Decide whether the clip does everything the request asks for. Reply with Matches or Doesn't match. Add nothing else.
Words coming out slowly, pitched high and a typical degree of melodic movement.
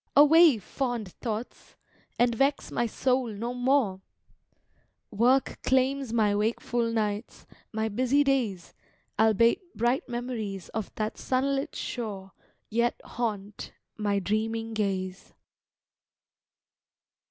Matches